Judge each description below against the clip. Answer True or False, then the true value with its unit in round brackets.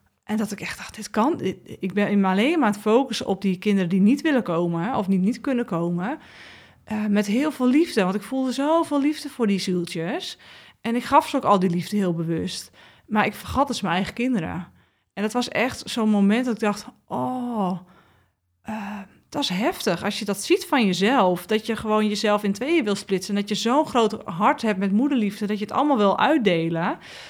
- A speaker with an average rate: False (215 wpm)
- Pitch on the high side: True (210 Hz)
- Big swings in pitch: False (4.5 semitones)